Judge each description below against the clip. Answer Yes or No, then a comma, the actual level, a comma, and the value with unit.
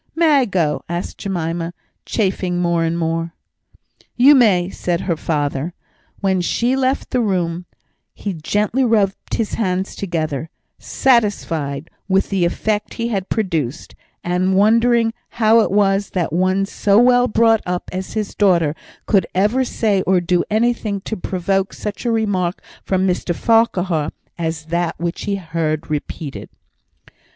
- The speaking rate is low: No, average, 145 wpm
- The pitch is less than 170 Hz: No, high, 190 Hz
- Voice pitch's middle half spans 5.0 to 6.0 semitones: No, average, 4.2 semitones